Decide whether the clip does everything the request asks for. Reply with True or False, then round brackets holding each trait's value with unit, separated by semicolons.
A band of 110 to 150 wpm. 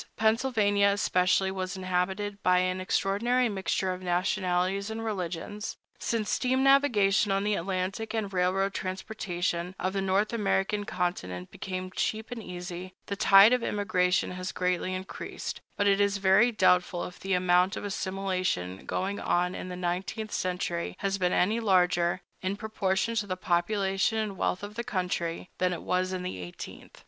False (160 wpm)